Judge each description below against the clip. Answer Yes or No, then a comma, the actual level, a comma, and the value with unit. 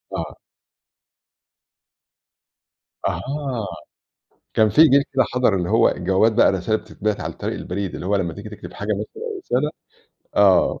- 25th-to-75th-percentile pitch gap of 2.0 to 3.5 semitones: No, average, 4.8 semitones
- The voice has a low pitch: Yes, low, 105 Hz